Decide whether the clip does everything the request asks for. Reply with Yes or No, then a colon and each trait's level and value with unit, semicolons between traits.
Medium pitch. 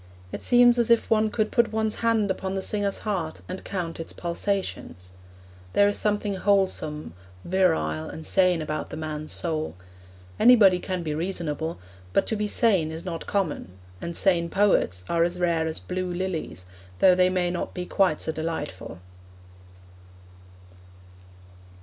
Yes: medium, 180 Hz